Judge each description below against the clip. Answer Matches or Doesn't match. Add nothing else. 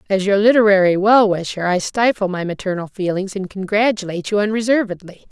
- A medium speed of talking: Matches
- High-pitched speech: Matches